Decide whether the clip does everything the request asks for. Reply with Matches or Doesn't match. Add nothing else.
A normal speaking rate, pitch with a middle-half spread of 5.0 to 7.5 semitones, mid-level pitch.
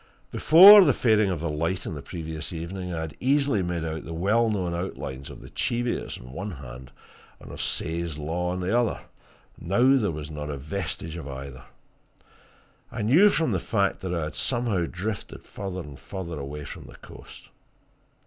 Doesn't match